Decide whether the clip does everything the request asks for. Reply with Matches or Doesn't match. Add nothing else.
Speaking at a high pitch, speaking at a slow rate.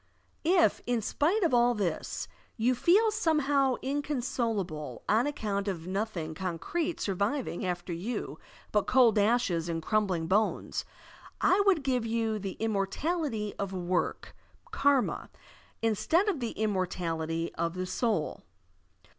Matches